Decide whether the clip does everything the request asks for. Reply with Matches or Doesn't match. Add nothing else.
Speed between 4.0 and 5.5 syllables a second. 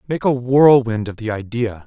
Matches